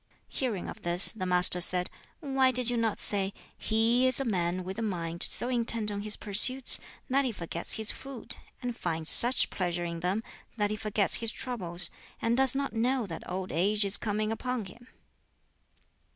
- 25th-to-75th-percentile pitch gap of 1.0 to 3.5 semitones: No, average, 5.0 semitones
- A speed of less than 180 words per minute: No, average, 185 wpm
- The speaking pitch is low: No, high, 215 Hz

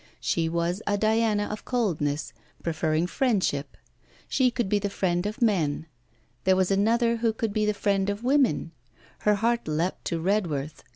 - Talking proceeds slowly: No, average, 165 wpm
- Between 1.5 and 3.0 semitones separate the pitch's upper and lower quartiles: No, average, 4.8 semitones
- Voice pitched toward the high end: Yes, high, 200 Hz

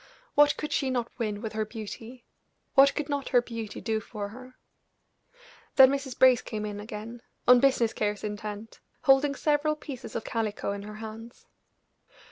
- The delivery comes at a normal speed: Yes, average, 165 wpm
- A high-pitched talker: Yes, high, 230 Hz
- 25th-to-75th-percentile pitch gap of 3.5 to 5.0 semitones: Yes, average, 3.8 semitones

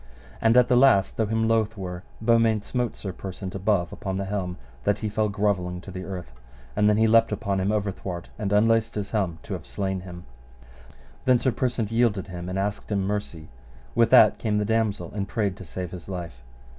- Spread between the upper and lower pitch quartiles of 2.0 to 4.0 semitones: Yes, average, 3.0 semitones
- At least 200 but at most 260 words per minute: Yes, fast, 205 wpm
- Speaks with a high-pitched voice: No, low, 100 Hz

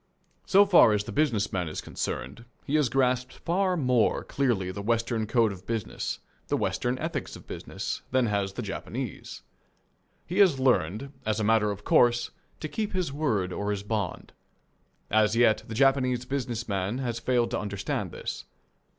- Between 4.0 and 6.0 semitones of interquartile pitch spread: Yes, average, 4.5 semitones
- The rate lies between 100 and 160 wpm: No, average, 170 wpm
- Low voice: Yes, low, 120 Hz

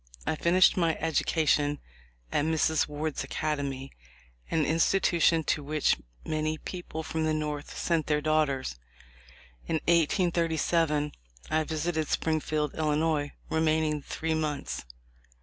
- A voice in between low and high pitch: Yes, medium, 155 Hz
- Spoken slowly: Yes, slow, 115 wpm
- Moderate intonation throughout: No, narrow, 1.4 semitones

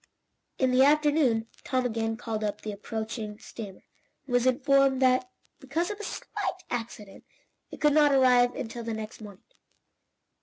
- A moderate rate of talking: Yes, average, 155 wpm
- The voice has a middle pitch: No, high, 245 Hz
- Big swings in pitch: No, average, 3.7 semitones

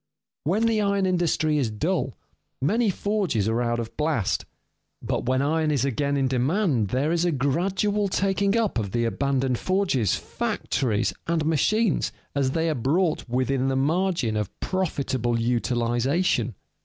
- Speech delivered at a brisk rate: No, average, 150 wpm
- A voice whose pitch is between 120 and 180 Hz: Yes, medium, 140 Hz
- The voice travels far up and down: Yes, wide, 6.9 semitones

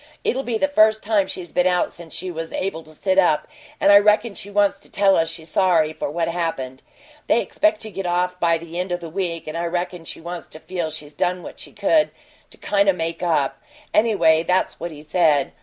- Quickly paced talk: Yes, fast, 235 wpm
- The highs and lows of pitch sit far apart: No, average, 3.3 semitones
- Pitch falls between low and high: Yes, medium, 175 Hz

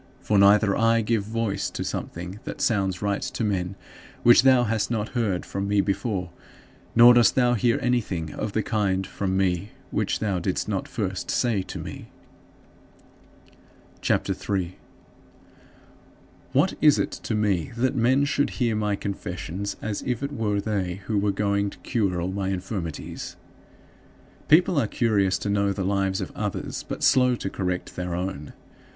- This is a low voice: Yes, low, 100 Hz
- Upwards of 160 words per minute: Yes, average, 170 wpm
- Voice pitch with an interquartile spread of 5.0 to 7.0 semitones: No, average, 3.4 semitones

